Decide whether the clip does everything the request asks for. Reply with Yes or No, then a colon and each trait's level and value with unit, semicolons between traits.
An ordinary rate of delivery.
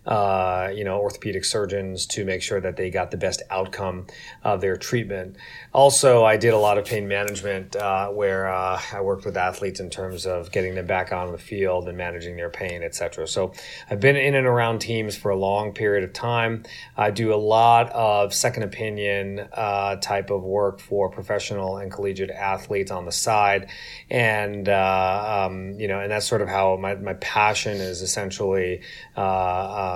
Yes: average, 190 wpm